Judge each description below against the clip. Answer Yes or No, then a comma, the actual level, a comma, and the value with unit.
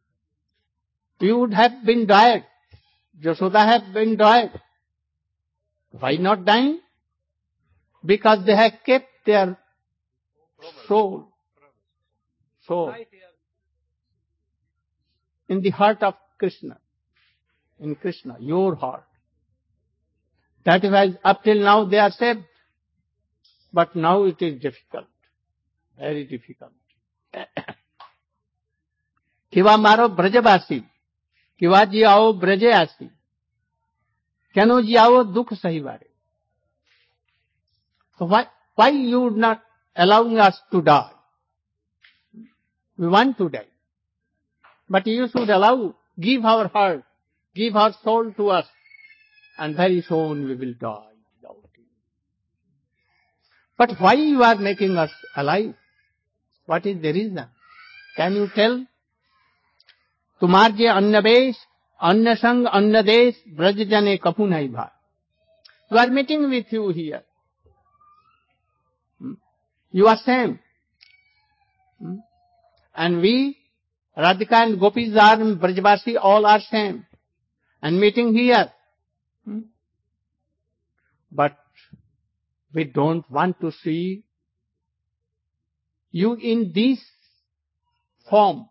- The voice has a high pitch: Yes, high, 195 Hz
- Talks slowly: Yes, slow, 95 wpm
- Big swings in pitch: Yes, wide, 7.7 semitones